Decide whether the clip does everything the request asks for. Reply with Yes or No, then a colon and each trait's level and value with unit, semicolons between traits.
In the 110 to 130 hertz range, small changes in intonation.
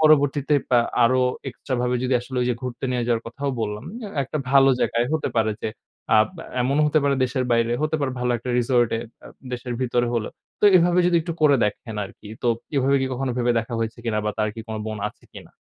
No: low, 125 Hz; average, 3.0 semitones